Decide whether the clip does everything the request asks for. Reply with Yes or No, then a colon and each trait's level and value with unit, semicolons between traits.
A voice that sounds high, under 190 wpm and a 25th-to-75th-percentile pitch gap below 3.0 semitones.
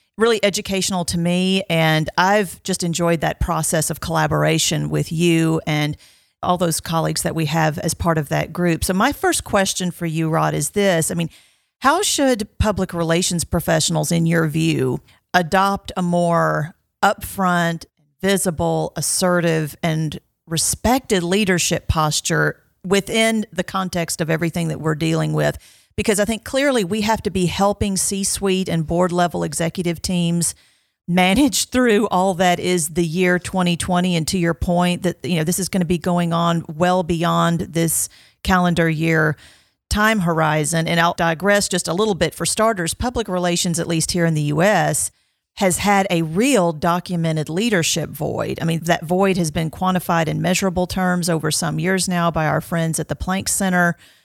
No: medium, 175 Hz; average, 170 wpm; narrow, 2.5 semitones